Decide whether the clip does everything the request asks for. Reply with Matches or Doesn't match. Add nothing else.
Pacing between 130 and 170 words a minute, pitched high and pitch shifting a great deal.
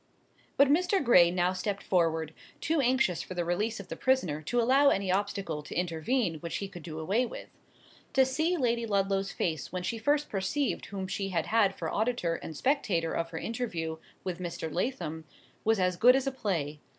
Doesn't match